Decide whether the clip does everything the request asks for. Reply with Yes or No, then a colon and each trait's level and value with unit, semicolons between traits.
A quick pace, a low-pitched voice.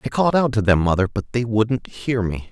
Yes: fast, 265 wpm; low, 115 Hz